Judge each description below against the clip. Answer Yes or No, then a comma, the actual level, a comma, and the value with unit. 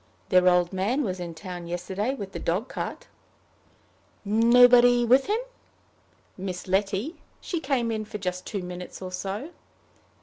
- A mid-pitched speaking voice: No, high, 200 Hz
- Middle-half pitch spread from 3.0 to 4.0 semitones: No, average, 5.0 semitones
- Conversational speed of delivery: Yes, average, 155 wpm